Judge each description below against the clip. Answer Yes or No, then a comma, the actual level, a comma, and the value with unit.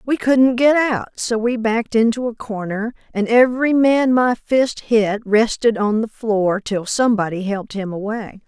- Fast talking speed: No, average, 175 wpm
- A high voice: Yes, high, 225 Hz